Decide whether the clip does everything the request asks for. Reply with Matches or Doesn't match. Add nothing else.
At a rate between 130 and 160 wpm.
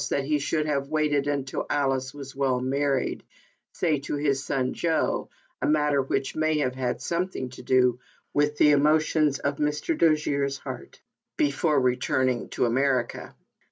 Matches